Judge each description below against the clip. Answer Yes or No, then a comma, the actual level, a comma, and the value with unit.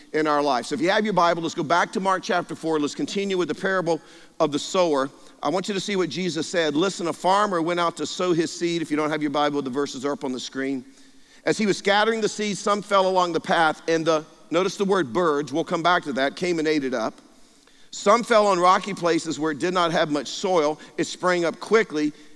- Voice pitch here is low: No, medium, 170 Hz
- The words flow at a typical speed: No, fast, 260 wpm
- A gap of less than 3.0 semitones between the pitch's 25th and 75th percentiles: No, average, 4.1 semitones